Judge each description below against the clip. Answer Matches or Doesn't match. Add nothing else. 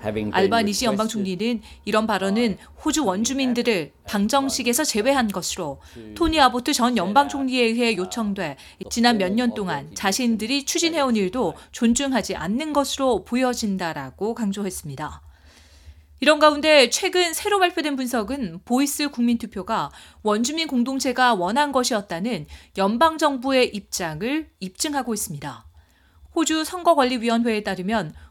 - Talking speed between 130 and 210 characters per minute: Doesn't match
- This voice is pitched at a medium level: Doesn't match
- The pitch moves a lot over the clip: Matches